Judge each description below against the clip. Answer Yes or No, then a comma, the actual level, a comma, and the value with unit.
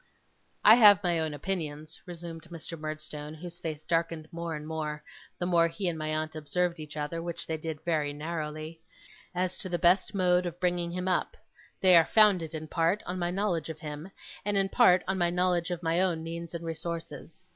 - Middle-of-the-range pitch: Yes, medium, 170 Hz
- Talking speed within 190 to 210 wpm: Yes, average, 200 wpm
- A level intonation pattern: Yes, narrow, 2.3 semitones